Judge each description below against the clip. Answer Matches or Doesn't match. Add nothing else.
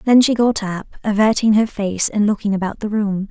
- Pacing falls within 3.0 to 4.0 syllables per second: Doesn't match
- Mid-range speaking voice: Doesn't match